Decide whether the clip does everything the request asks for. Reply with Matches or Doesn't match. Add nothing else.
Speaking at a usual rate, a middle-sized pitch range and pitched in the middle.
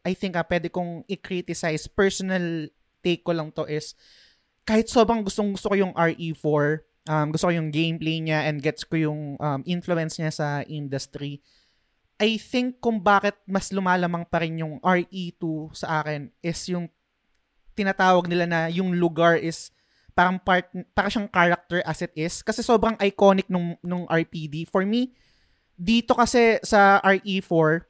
Doesn't match